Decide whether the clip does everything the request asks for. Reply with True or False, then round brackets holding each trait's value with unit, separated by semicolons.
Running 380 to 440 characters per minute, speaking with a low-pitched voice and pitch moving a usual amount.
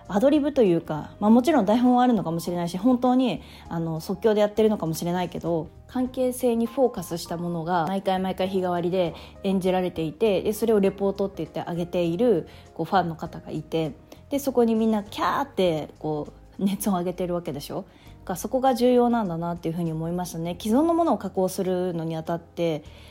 False (395 characters per minute; 185 Hz; 4.9 semitones)